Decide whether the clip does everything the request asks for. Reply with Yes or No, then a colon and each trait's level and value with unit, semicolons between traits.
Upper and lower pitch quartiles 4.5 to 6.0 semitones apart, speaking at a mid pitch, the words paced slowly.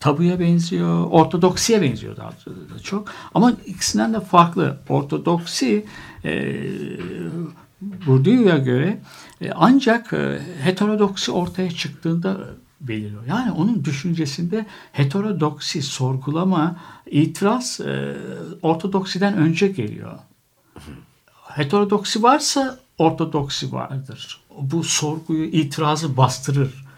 Yes: wide, 5.4 semitones; medium, 165 Hz; slow, 85 wpm